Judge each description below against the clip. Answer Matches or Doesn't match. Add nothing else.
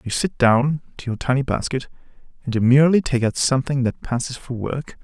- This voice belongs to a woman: Doesn't match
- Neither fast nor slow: Matches